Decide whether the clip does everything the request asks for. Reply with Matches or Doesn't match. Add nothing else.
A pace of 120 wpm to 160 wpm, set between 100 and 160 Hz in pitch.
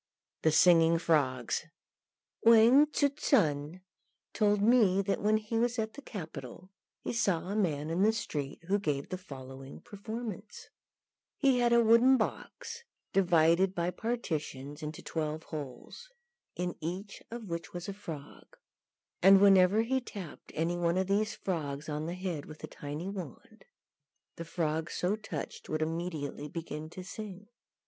Doesn't match